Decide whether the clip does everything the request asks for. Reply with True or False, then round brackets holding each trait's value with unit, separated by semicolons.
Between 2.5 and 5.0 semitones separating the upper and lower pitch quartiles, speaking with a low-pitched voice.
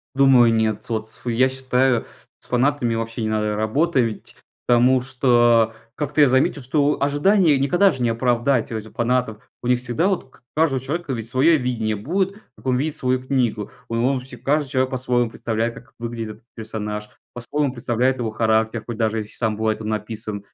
True (3.1 semitones; 125 Hz)